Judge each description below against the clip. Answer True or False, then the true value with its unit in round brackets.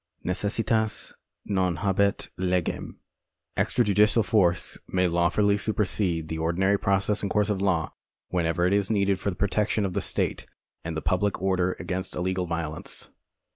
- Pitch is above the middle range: False (95 Hz)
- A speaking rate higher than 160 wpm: False (150 wpm)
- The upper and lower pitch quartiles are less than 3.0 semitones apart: True (2.5 semitones)